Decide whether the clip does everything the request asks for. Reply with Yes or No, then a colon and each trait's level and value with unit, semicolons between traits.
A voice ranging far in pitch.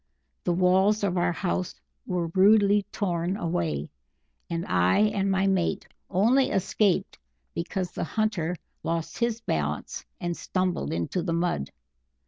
No: average, 3.0 semitones